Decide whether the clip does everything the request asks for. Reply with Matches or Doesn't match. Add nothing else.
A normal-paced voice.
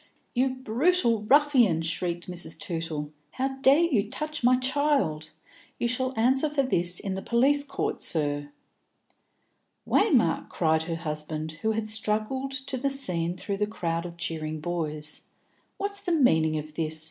Matches